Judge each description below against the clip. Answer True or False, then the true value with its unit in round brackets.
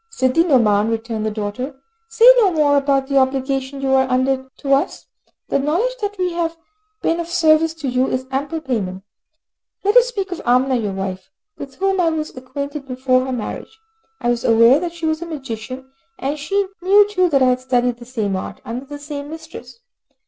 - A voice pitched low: False (275 Hz)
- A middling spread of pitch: True (4.5 semitones)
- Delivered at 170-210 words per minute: True (200 wpm)